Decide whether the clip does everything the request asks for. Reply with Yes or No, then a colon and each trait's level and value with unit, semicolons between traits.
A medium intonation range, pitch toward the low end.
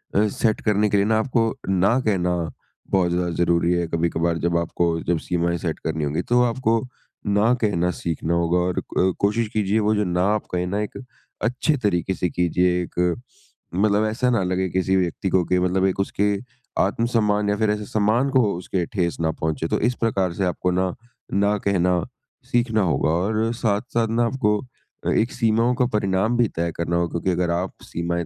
Yes: average, 3.7 semitones; very low, 95 Hz